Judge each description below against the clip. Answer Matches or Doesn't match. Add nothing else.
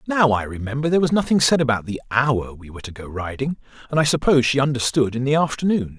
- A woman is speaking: Doesn't match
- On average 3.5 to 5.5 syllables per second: Doesn't match